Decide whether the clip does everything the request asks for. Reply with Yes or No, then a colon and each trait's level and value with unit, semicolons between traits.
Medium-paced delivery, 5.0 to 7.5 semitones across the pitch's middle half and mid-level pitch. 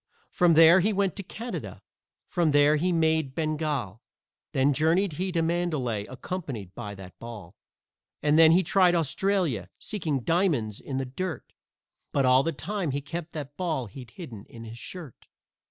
Yes: average, 165 wpm; average, 5.3 semitones; medium, 155 Hz